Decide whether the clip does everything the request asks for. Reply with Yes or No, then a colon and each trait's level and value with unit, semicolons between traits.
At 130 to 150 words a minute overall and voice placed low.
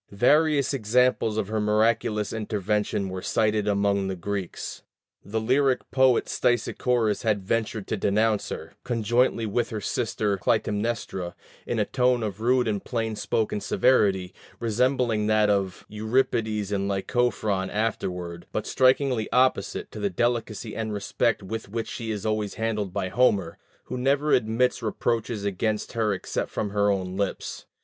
Yes: average, 145 wpm; low, 110 Hz